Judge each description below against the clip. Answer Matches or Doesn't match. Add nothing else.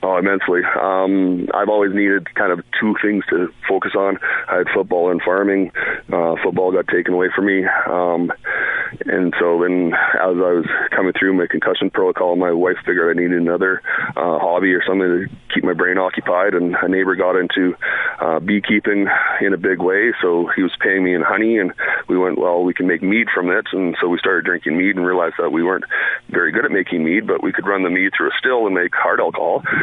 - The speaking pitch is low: Matches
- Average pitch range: Doesn't match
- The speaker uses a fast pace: Matches